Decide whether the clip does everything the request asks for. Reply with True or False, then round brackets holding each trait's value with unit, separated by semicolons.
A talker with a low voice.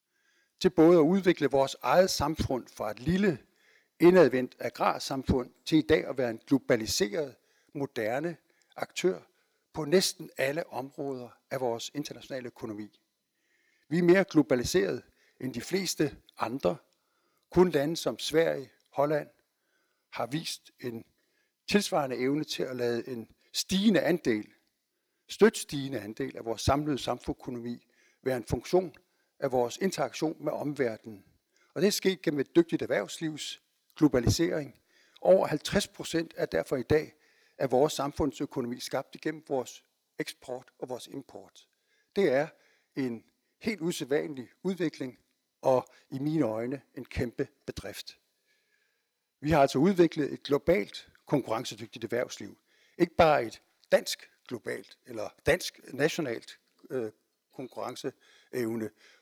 False (145 Hz)